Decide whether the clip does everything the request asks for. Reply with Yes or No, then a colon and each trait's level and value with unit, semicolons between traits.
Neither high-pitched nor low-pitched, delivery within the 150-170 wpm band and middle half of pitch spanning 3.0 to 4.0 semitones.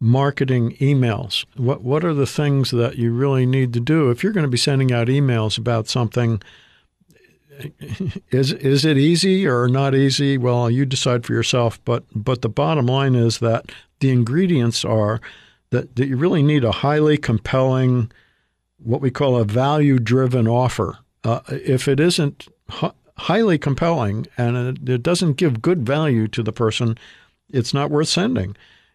No: low, 130 Hz; average, 160 wpm; average, 3.3 semitones